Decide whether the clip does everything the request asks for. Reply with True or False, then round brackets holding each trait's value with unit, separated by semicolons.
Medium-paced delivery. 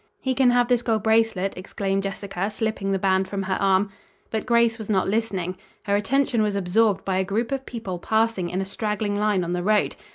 False (215 wpm)